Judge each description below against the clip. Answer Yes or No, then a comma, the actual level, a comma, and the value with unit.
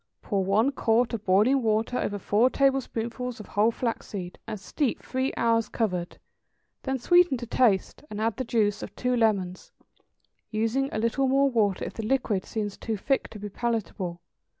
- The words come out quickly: No, average, 175 wpm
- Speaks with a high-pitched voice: Yes, high, 225 Hz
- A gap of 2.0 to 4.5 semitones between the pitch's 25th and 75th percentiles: Yes, average, 3.5 semitones